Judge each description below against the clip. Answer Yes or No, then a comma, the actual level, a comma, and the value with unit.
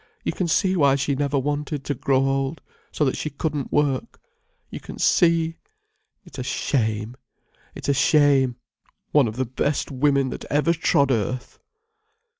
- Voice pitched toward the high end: No, medium, 140 Hz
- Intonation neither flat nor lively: No, narrow, 2.2 semitones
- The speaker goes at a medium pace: Yes, average, 160 wpm